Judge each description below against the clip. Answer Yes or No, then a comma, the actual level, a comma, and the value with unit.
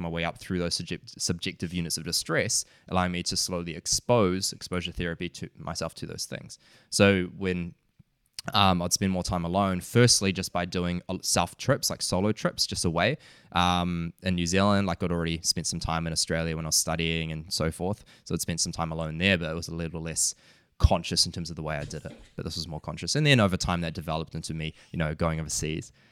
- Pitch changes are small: Yes, narrow, 2.3 semitones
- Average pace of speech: No, fast, 225 wpm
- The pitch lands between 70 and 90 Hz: Yes, very low, 85 Hz